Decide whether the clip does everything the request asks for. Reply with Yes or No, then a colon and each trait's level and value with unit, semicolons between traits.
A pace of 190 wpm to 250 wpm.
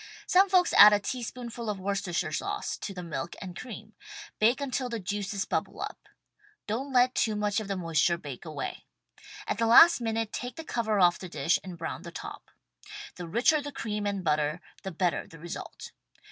Yes: average, 195 wpm